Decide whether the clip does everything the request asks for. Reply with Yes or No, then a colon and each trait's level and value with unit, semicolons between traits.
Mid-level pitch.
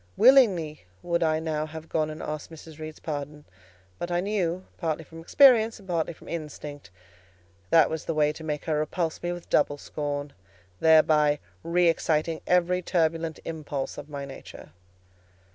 Yes: medium, 160 Hz